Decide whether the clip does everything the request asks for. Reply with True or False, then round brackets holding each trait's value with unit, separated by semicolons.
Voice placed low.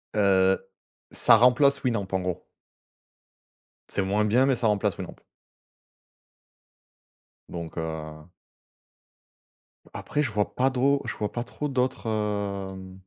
True (105 Hz)